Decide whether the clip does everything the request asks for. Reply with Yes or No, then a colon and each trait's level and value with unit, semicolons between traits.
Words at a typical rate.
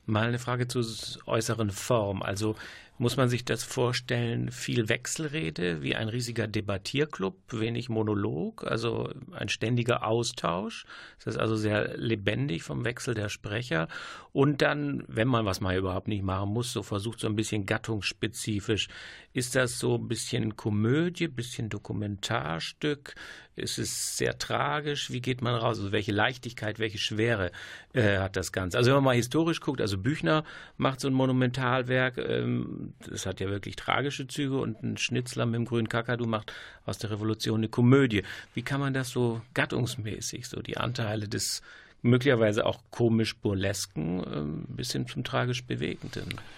Yes: average, 160 wpm